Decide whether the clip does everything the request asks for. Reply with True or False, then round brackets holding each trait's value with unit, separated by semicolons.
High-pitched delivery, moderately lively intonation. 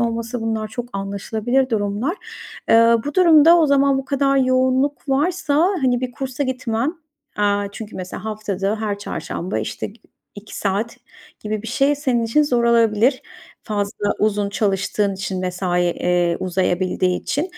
True (225 Hz; 4.6 semitones)